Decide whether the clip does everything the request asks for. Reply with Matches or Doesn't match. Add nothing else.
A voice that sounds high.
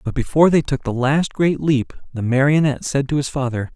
Doesn't match